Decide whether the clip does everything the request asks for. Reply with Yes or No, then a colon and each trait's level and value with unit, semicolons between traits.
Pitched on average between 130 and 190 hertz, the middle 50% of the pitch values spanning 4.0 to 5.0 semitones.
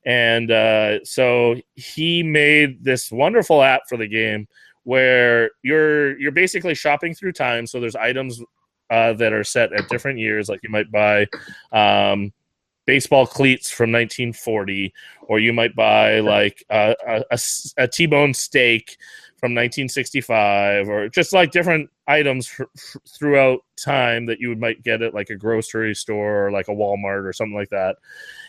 No: low, 120 Hz; average, 4.3 semitones